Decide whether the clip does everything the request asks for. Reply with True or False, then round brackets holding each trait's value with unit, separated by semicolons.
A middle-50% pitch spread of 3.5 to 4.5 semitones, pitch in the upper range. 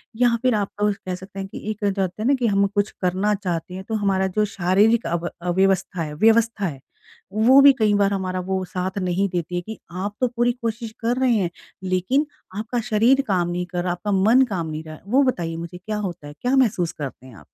True (4.0 semitones; 195 Hz)